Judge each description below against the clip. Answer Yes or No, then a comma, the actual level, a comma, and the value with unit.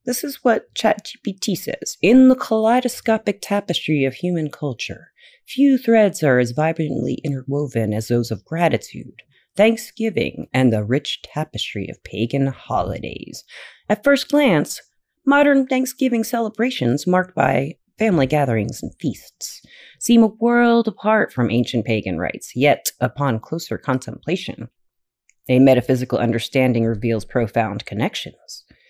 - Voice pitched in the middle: Yes, medium, 160 Hz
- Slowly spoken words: Yes, slow, 125 wpm